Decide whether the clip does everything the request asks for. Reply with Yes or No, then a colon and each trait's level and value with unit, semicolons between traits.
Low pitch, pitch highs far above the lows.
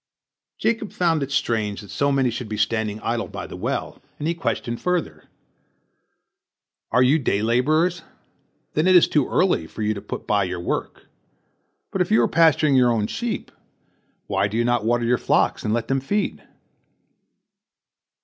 Yes: low, 120 Hz; wide, 6.3 semitones